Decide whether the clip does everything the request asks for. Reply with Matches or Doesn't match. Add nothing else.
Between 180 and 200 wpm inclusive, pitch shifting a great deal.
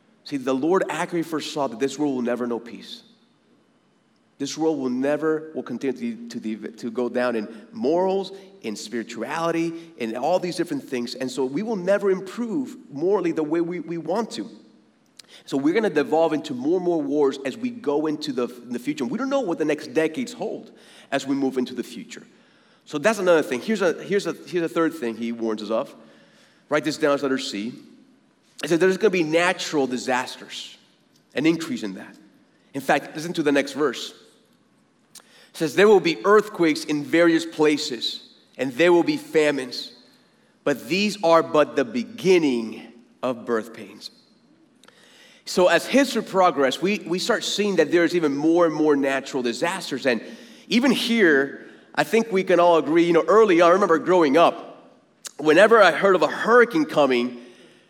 Matches